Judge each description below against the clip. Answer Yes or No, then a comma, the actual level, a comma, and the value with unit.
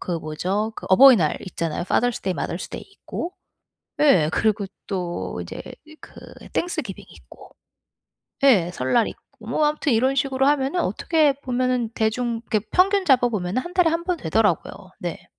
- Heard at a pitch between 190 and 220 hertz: No, high, 245 Hz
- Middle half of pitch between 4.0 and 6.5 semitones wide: No, wide, 7.5 semitones